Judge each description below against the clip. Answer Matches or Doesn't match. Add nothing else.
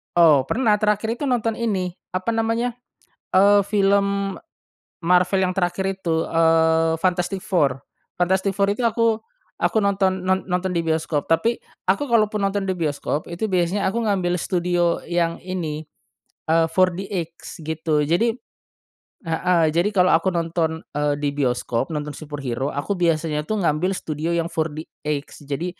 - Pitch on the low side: Doesn't match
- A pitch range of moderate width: Matches